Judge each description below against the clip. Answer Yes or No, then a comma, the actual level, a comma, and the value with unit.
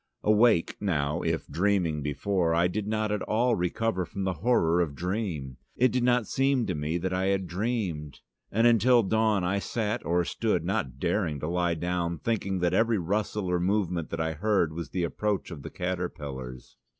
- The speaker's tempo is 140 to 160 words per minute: No, average, 185 wpm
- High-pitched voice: No, very low, 90 Hz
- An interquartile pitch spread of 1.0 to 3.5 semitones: No, average, 4.2 semitones